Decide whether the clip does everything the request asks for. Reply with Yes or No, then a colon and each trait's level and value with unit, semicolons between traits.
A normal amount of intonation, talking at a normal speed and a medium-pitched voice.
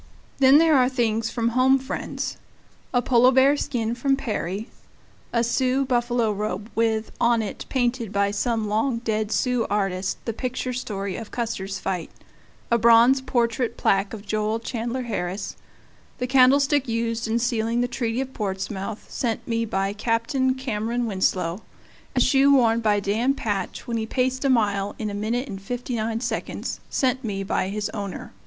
No: average, 3.1 semitones; average, 155 wpm; high, 230 Hz